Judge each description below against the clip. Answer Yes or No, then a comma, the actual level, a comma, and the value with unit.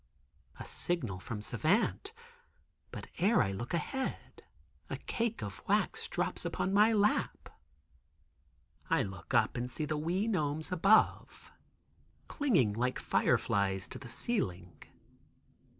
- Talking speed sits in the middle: No, slow, 120 wpm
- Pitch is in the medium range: Yes, medium, 155 Hz